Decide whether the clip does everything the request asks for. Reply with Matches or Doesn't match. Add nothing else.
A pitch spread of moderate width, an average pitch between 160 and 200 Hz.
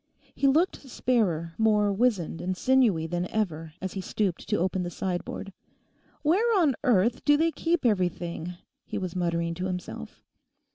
Doesn't match